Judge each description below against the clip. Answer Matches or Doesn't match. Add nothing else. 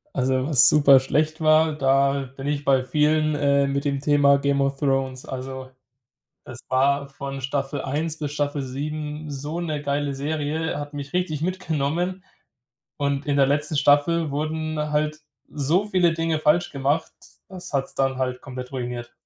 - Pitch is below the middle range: Doesn't match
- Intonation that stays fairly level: Matches